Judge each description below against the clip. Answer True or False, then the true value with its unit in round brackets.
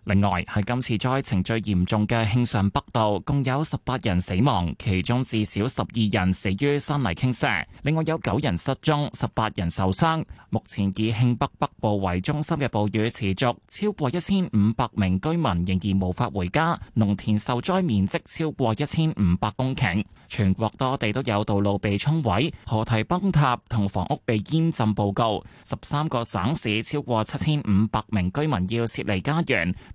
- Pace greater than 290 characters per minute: False (265 characters per minute)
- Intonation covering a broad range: True (5.8 semitones)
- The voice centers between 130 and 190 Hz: False (110 Hz)